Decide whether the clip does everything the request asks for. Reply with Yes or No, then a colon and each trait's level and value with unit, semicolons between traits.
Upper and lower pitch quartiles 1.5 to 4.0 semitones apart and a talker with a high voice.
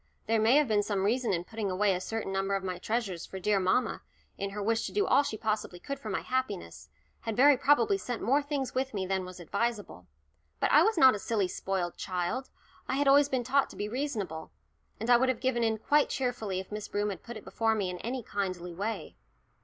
No: average, 5.1 semitones; high, 220 Hz